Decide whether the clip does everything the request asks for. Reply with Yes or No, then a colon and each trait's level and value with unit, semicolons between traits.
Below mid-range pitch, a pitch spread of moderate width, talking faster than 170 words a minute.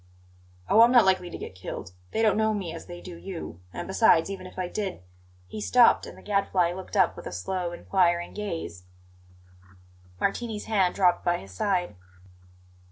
No: medium, 185 Hz; average, 3.1 semitones; average, 185 wpm